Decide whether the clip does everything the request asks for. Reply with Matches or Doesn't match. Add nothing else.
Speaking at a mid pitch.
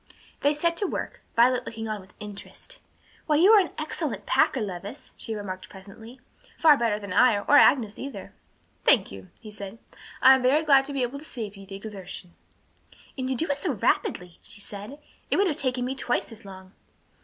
Doesn't match